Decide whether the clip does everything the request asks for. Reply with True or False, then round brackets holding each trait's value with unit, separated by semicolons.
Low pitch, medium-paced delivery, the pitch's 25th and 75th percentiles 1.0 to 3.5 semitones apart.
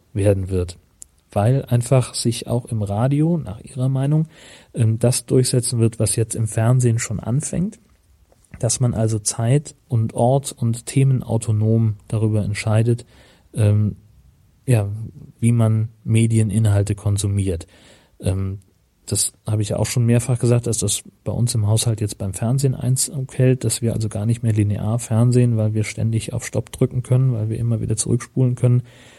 True (115 Hz; 155 wpm; 2.8 semitones)